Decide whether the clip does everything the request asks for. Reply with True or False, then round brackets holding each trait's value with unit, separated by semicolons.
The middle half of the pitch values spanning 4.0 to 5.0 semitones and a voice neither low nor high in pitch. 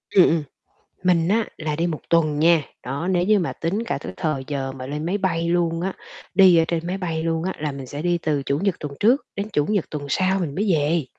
False (3.6 semitones; 165 Hz)